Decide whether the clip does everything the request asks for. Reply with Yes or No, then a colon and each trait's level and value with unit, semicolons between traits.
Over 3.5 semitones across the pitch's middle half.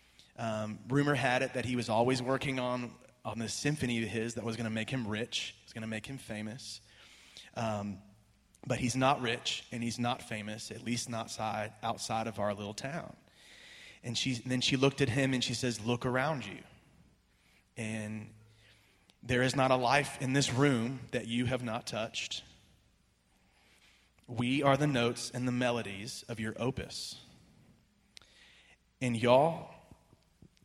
No: narrow, 2.6 semitones